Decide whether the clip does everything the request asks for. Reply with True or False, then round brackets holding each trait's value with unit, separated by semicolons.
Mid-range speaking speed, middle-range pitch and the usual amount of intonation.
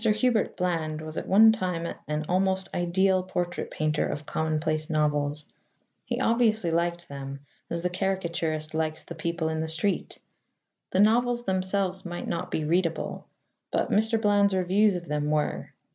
True (155 wpm; 175 Hz; 3.6 semitones)